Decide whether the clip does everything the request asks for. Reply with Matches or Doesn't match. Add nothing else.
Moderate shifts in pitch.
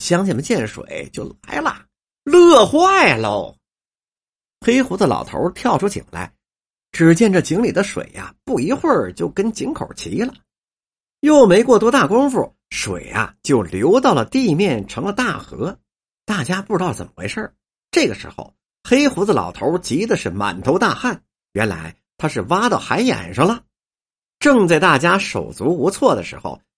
Doesn't match